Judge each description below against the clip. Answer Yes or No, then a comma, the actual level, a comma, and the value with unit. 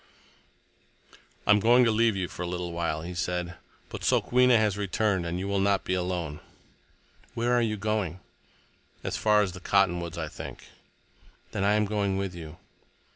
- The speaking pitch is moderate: No, very low, 95 Hz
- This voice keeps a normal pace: Yes, average, 180 wpm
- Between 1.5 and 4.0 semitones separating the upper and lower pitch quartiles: Yes, average, 3.4 semitones